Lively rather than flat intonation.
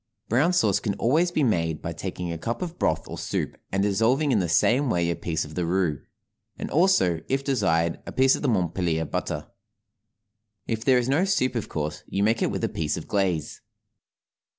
Yes: wide, 7.7 semitones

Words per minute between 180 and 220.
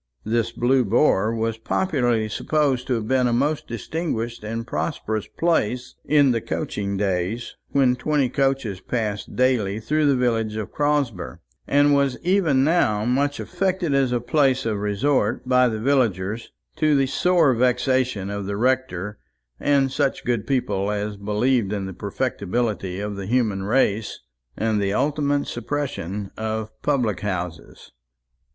No: average, 145 wpm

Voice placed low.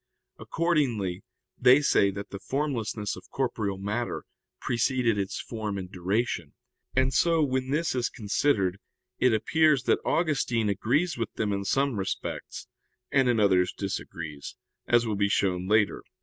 Yes: low, 115 Hz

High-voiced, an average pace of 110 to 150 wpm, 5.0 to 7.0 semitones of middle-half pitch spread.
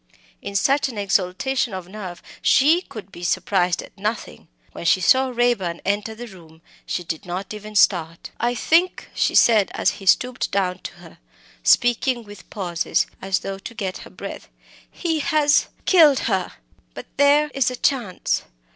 No: high, 210 Hz; average, 165 wpm; wide, 5.6 semitones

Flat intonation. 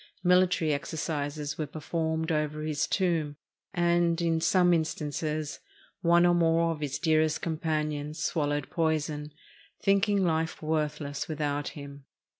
Yes: narrow, 2.0 semitones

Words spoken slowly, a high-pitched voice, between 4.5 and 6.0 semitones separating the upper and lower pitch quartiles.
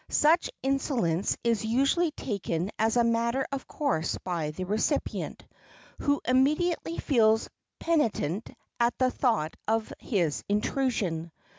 Yes: slow, 120 wpm; high, 230 Hz; wide, 5.4 semitones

